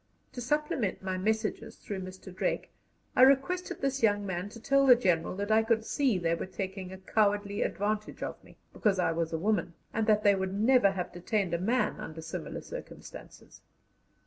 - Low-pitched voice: No, high, 205 Hz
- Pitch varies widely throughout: No, average, 3.6 semitones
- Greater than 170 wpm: Yes, average, 190 wpm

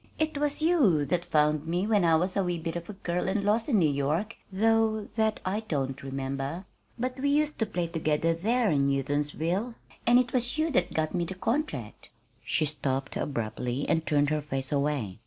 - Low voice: No, medium, 175 Hz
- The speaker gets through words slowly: No, fast, 205 wpm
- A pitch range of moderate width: No, wide, 7.1 semitones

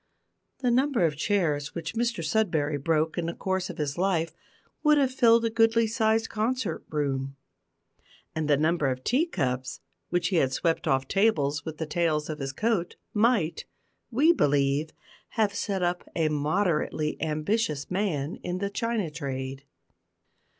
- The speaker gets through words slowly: No, average, 155 wpm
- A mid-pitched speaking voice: Yes, medium, 170 Hz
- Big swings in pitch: Yes, wide, 6.6 semitones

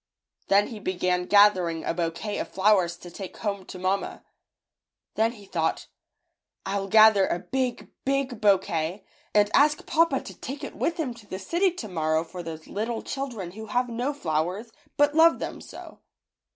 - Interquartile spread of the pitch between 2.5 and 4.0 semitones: No, wide, 5.5 semitones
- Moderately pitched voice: No, high, 205 Hz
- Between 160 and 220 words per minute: Yes, average, 170 wpm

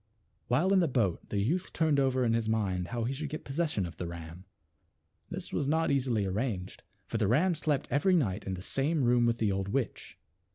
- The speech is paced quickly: Yes, fast, 215 wpm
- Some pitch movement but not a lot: No, wide, 6.7 semitones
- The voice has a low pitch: Yes, low, 120 Hz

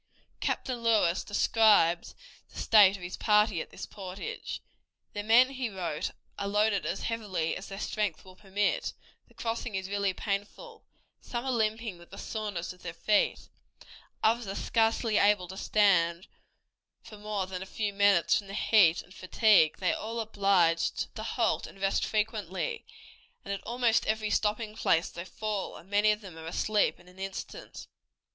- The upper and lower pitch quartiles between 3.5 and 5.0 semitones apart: No, average, 2.8 semitones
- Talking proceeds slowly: No, average, 170 wpm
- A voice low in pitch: No, high, 205 Hz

